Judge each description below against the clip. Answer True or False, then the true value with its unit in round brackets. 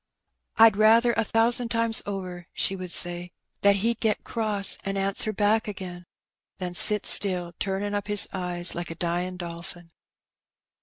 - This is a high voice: True (195 Hz)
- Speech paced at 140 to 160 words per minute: True (155 wpm)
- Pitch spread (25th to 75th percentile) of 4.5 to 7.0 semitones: False (3.4 semitones)